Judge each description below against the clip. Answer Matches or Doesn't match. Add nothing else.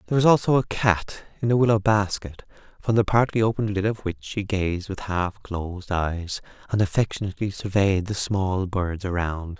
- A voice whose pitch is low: Matches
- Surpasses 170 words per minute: Matches